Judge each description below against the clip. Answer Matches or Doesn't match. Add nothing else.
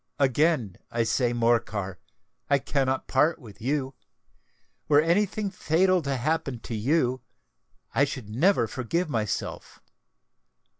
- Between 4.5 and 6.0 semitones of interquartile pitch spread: Matches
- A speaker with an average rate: Doesn't match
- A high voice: Doesn't match